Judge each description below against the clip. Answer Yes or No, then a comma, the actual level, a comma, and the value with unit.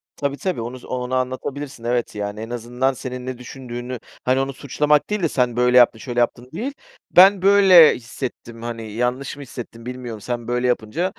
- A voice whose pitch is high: No, low, 125 Hz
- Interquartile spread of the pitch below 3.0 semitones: Yes, narrow, 2.6 semitones